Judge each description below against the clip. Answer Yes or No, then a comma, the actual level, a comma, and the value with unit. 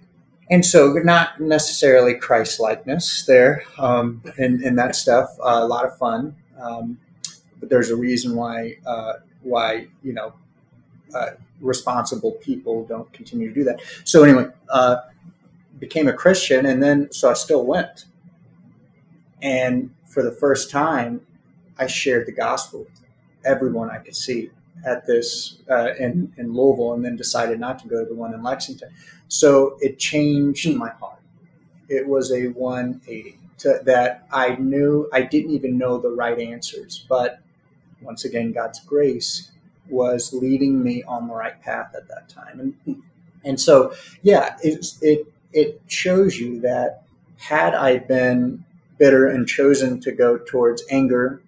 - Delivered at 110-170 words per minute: Yes, average, 155 wpm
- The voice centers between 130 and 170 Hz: Yes, low, 135 Hz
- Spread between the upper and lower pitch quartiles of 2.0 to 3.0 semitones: No, average, 4.6 semitones